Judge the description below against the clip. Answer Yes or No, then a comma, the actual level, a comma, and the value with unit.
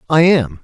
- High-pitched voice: No, medium, 140 Hz